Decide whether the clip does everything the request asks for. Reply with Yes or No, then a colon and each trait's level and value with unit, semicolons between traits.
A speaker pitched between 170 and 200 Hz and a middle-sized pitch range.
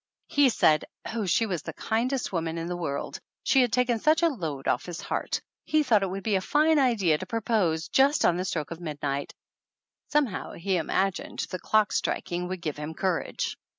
No: high, 190 Hz; wide, 6.4 semitones